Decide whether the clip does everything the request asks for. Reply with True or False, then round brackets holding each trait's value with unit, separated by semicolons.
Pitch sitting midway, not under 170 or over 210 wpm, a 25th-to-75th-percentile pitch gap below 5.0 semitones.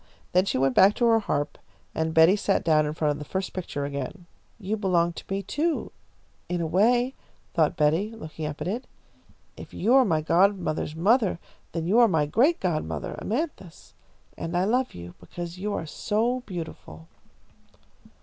False (180 Hz; 180 wpm; 5.3 semitones)